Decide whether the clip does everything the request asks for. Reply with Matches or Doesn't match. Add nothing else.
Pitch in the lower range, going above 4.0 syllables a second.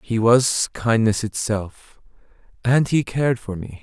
Doesn't match